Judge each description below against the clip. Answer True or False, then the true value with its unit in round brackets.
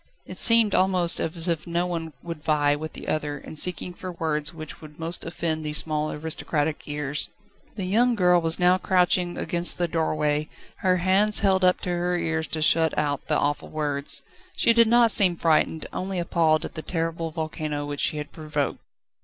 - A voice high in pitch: False (165 Hz)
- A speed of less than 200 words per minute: True (185 wpm)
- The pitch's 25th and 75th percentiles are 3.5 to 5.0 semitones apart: False (2.7 semitones)